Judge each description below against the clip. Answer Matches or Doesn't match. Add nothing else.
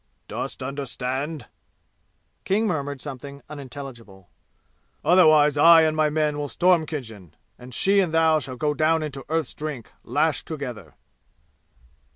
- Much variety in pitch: Doesn't match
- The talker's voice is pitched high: Doesn't match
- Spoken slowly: Matches